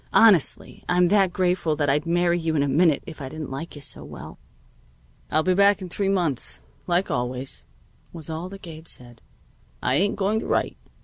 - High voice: No, medium, 170 Hz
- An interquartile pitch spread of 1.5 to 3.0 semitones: No, average, 4.1 semitones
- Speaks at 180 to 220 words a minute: Yes, average, 195 wpm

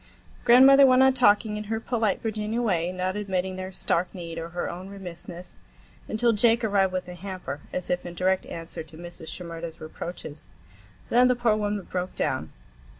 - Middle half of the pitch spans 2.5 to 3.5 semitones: No, average, 4.0 semitones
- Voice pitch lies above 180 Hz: Yes, high, 190 Hz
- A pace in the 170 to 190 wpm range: Yes, average, 180 wpm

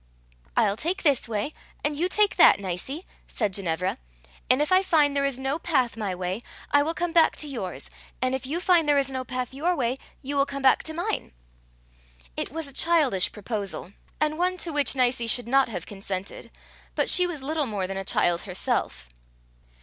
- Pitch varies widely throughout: Yes, wide, 6.9 semitones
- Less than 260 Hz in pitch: No, very high, 270 Hz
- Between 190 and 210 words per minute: Yes, average, 200 wpm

